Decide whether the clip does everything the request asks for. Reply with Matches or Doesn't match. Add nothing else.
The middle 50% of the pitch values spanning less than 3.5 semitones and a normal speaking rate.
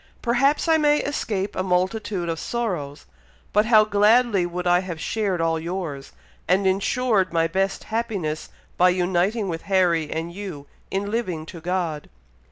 Doesn't match